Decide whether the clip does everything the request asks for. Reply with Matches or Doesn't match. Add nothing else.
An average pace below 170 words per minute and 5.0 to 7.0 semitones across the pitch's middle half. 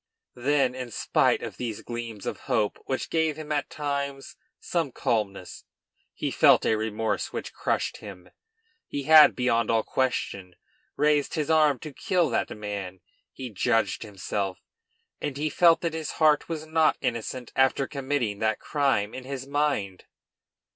Matches